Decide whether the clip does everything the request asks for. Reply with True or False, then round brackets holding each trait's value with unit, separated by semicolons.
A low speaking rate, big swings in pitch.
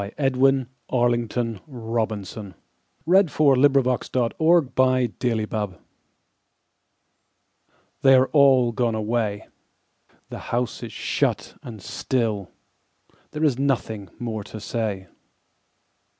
False (95 wpm; 3.4 semitones)